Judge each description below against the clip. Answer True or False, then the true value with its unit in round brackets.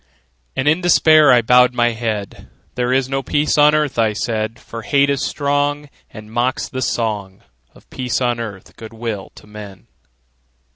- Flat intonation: False (4.3 semitones)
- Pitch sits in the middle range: False (120 Hz)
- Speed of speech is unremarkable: True (175 wpm)